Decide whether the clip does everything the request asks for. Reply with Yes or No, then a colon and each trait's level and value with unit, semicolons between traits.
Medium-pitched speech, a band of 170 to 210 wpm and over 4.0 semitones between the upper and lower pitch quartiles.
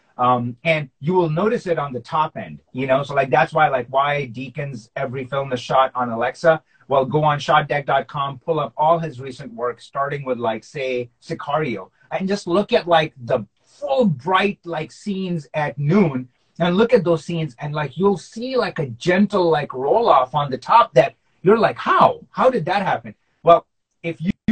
Yes: medium, 150 Hz; average, 200 wpm; average, 4.4 semitones